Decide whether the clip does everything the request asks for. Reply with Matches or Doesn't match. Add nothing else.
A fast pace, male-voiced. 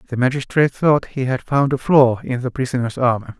Matches